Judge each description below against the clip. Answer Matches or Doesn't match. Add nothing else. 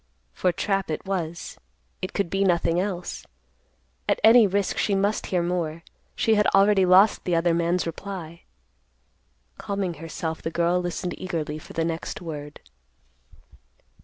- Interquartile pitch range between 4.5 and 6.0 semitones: Doesn't match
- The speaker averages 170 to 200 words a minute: Doesn't match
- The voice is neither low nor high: Matches